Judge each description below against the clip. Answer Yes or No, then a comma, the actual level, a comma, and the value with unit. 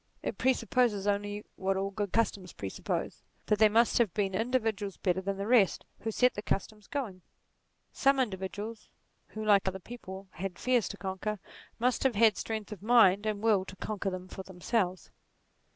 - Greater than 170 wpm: Yes, average, 180 wpm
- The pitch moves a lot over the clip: No, average, 2.8 semitones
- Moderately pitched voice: No, high, 205 Hz